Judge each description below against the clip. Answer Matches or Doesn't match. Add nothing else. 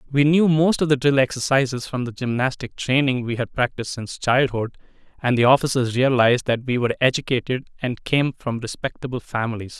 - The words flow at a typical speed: Matches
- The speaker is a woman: Doesn't match